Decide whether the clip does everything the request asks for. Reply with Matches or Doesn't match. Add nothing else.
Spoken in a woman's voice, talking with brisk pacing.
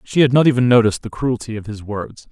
Doesn't match